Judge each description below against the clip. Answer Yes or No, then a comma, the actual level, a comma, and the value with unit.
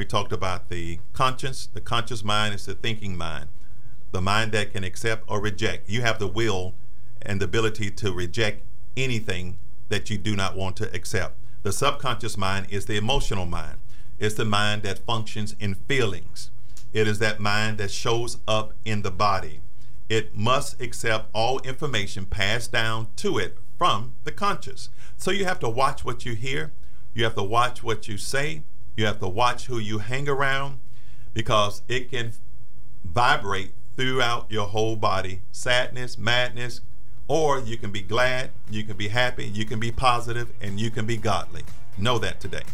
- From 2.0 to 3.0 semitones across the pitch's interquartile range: Yes, average, 2.7 semitones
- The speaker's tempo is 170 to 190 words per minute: Yes, average, 175 wpm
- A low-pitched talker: Yes, low, 115 Hz